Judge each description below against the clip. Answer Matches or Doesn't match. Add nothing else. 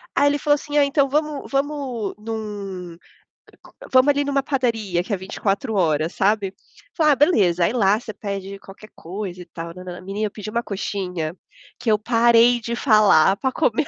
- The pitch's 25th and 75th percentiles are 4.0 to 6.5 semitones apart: Matches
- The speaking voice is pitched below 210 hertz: Doesn't match